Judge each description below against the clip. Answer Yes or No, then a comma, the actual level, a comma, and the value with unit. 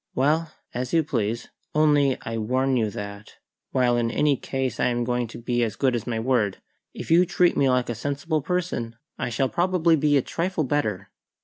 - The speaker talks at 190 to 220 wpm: Yes, average, 200 wpm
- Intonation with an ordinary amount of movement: Yes, average, 4.4 semitones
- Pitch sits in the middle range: No, low, 130 Hz